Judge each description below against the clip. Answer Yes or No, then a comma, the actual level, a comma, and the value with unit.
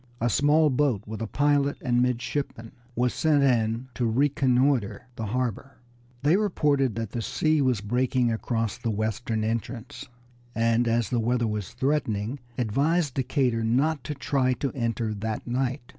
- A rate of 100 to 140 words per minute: No, average, 155 wpm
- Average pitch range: Yes, average, 3.4 semitones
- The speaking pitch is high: No, low, 125 Hz